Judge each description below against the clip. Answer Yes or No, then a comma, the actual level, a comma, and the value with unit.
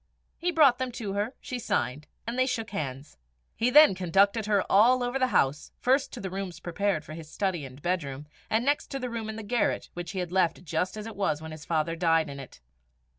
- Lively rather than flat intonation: Yes, wide, 6.6 semitones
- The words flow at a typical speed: No, fast, 230 wpm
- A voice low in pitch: No, high, 195 Hz